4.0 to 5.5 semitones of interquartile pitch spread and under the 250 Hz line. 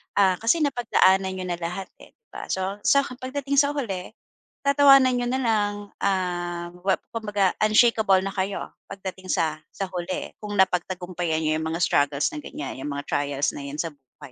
Yes: average, 4.7 semitones; high, 190 Hz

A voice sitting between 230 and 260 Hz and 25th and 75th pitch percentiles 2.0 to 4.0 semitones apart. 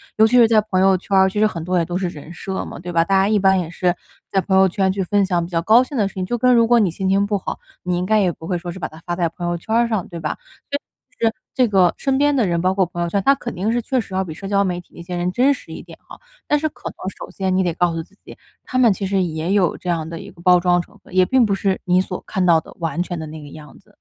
No: high, 190 Hz; average, 3.2 semitones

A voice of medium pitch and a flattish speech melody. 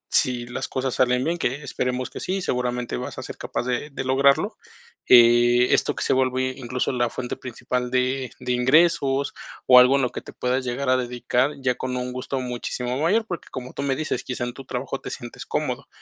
No: low, 125 Hz; narrow, 1.5 semitones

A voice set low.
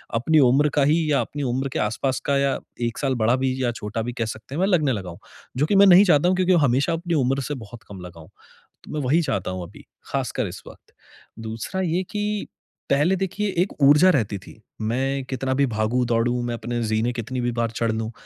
Yes: low, 130 Hz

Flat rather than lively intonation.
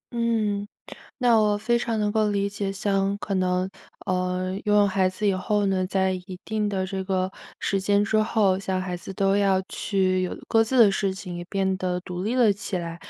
Yes: narrow, 1.9 semitones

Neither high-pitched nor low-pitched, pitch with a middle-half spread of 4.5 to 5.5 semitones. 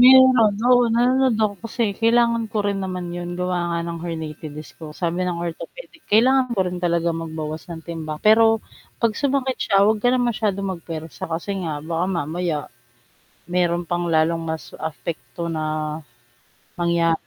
Yes: medium, 175 Hz; average, 5.2 semitones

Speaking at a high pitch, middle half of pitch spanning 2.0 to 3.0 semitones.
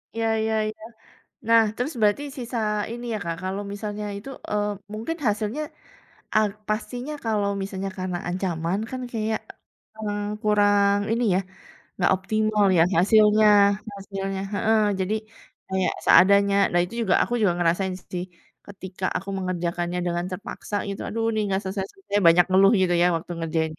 Yes: high, 200 Hz; average, 2.7 semitones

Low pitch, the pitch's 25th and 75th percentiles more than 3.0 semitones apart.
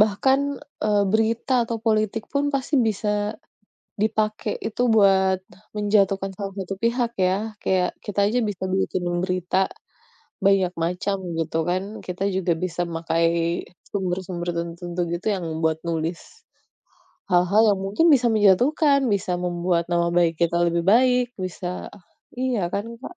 No: high, 195 Hz; average, 3.6 semitones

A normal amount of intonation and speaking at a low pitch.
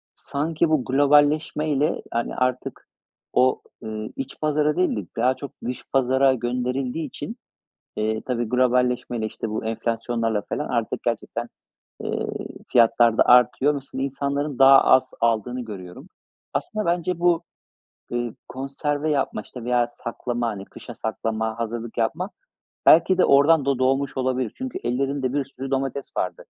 Yes: average, 3.4 semitones; low, 130 Hz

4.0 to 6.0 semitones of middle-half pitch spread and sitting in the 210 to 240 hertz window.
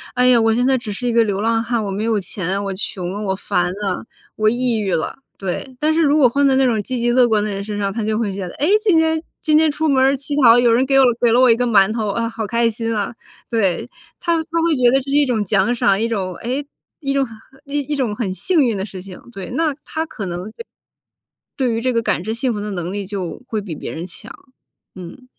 Yes: average, 4.6 semitones; high, 230 Hz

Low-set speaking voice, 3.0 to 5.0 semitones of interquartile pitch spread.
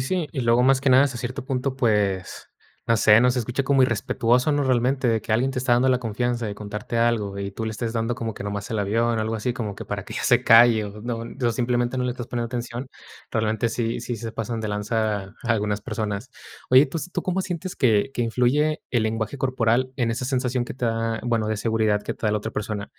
No: low, 115 Hz; narrow, 2.5 semitones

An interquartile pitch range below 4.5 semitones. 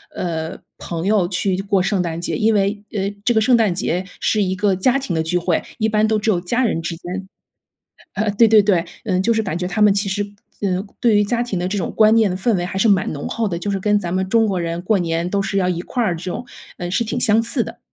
Yes: average, 3.2 semitones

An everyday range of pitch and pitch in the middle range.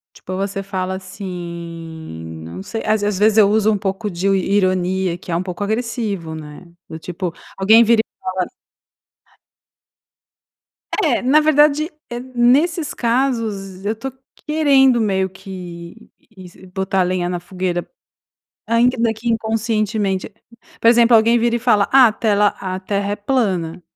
No: average, 4.0 semitones; high, 200 Hz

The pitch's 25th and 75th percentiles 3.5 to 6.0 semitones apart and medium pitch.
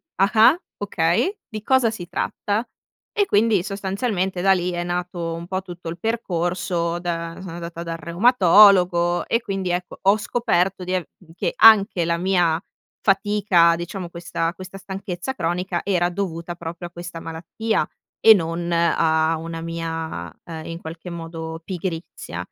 No: average, 2.7 semitones; medium, 175 Hz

